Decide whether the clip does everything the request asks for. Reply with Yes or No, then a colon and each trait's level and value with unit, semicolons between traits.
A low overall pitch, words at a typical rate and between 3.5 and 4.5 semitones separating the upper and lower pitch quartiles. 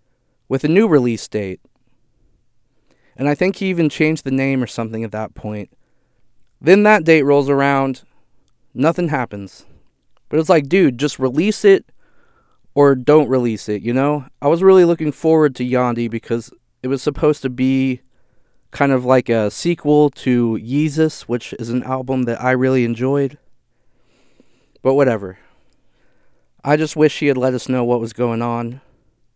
Yes: low, 130 Hz; average, 165 wpm; average, 3.9 semitones